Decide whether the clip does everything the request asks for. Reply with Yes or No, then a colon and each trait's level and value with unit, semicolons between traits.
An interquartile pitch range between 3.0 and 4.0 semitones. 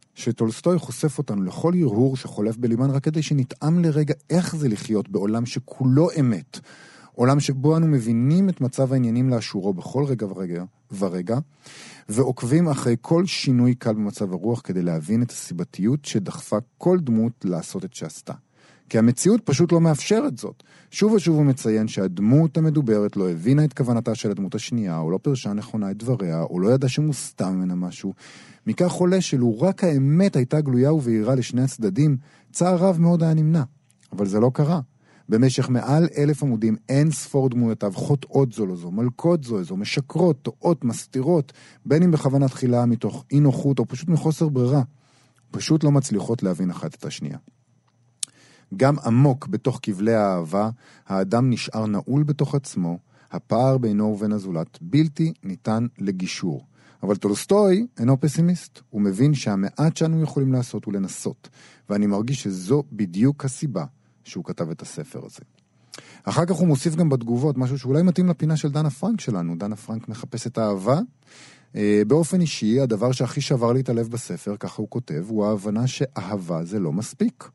No: wide, 5.6 semitones